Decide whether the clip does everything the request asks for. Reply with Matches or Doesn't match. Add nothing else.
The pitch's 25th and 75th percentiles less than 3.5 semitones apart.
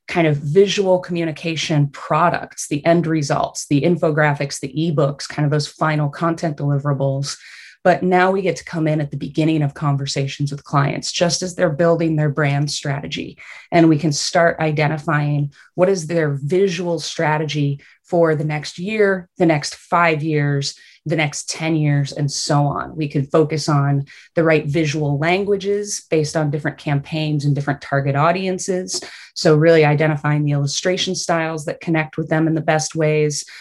Matches